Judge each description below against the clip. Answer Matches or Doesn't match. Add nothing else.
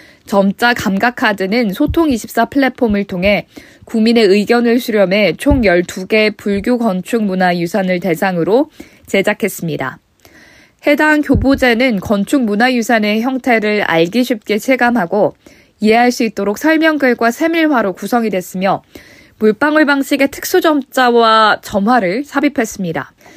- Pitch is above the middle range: Matches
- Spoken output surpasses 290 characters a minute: Doesn't match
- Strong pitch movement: Doesn't match